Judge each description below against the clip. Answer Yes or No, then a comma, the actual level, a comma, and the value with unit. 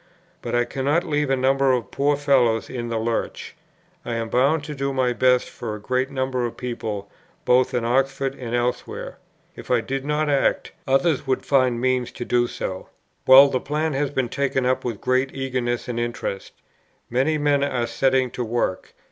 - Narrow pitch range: Yes, narrow, 2.2 semitones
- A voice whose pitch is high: No, low, 130 Hz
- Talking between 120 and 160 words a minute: No, average, 190 wpm